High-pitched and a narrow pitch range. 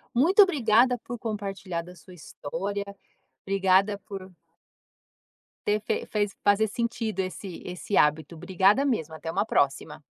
No: high, 200 Hz; average, 3.4 semitones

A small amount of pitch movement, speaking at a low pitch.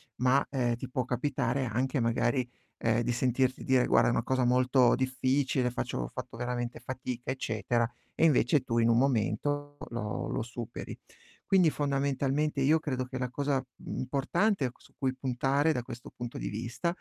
Yes: narrow, 2.3 semitones; low, 130 Hz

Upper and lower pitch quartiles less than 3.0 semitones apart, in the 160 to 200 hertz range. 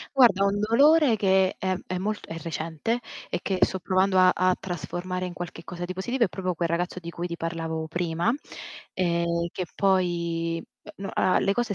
Yes: narrow, 2.4 semitones; medium, 185 Hz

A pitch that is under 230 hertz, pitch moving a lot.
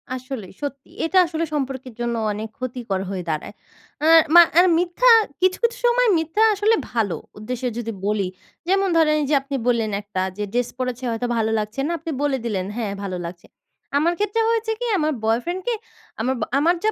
No: very high, 260 Hz; wide, 7.8 semitones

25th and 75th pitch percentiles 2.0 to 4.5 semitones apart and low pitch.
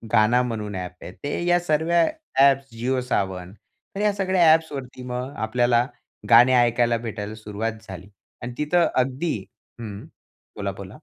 No: wide, 5.5 semitones; low, 125 Hz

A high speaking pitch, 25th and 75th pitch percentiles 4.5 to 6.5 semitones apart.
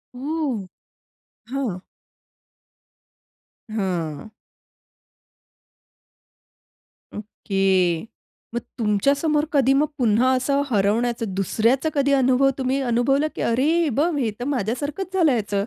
Yes: very high, 250 Hz; average, 4.9 semitones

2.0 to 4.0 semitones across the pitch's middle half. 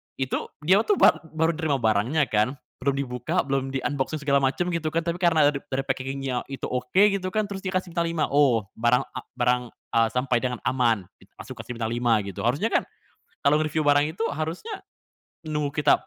No: average, 4.4 semitones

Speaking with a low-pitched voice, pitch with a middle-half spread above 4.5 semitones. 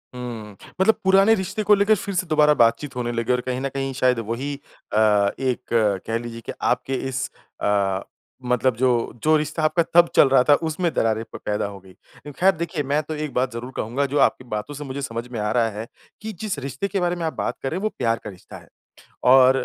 Yes: low, 130 Hz; average, 5.3 semitones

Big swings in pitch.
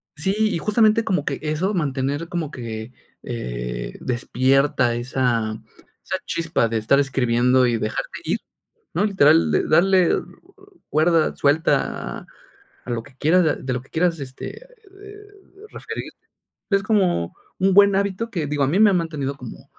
Yes: wide, 7.1 semitones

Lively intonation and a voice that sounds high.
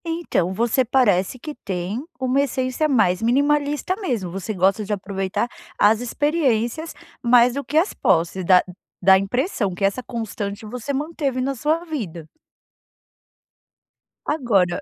Yes: wide, 6.3 semitones; high, 235 Hz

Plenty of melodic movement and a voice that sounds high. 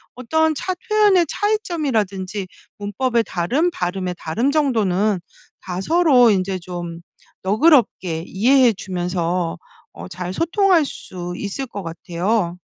Yes: wide, 7.7 semitones; high, 205 Hz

